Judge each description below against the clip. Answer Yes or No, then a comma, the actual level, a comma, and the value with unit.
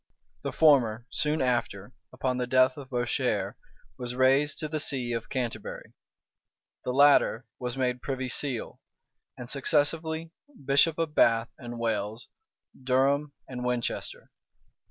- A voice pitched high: No, low, 130 Hz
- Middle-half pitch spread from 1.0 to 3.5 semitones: Yes, average, 2.8 semitones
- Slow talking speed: Yes, slow, 130 wpm